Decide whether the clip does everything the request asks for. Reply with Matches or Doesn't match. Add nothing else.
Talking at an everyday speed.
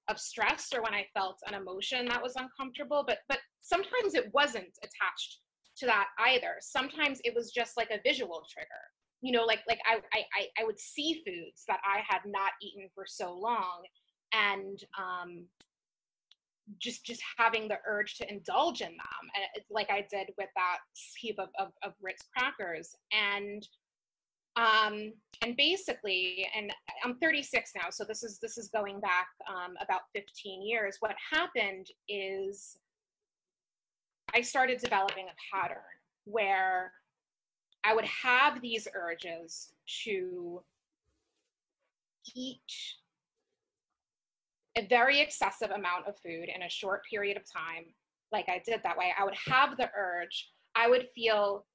Matches